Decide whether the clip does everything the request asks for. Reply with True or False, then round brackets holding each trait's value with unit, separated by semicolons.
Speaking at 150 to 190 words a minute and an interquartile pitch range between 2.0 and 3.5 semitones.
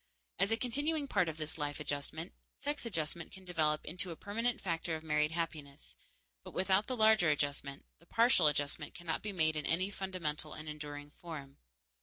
False (180 wpm; 4.6 semitones)